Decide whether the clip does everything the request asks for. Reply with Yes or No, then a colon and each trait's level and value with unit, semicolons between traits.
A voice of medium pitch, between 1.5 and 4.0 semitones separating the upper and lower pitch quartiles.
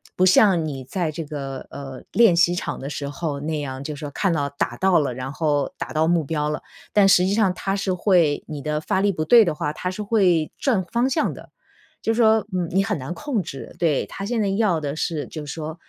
No: medium, 165 Hz; average, 4.8 semitones